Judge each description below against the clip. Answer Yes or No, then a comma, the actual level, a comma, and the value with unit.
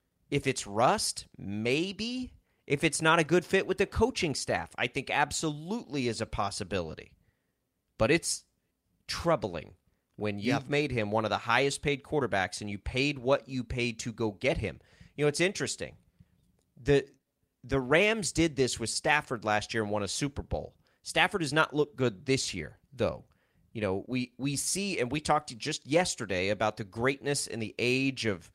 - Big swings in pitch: Yes, wide, 5.7 semitones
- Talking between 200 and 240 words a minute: No, average, 185 wpm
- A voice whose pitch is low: Yes, low, 130 Hz